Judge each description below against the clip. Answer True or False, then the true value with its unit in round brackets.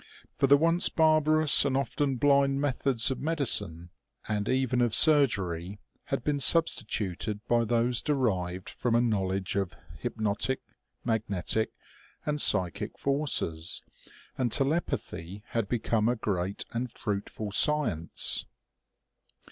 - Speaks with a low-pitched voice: True (120 Hz)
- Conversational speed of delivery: False (115 wpm)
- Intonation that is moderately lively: False (5.8 semitones)